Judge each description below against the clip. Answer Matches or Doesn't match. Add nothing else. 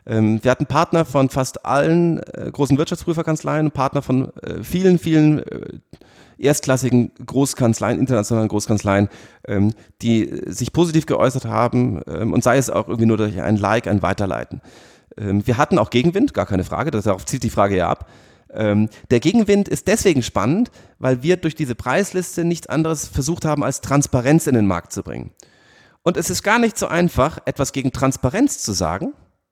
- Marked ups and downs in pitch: Matches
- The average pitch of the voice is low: Matches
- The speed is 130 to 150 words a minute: Doesn't match